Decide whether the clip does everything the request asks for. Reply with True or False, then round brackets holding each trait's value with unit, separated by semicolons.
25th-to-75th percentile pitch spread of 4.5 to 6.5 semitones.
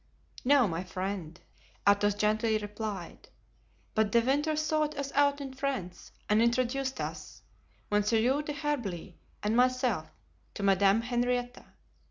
True (4.9 semitones)